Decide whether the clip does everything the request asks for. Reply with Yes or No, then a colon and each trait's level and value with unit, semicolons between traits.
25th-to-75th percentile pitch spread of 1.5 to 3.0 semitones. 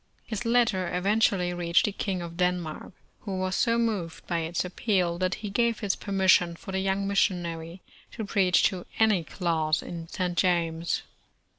Yes: average, 2.7 semitones